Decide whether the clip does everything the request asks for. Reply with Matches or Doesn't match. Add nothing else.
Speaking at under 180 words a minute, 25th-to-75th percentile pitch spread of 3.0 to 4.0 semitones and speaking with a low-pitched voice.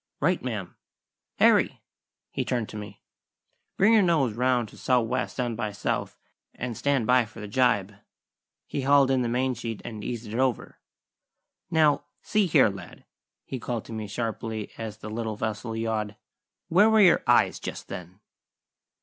Matches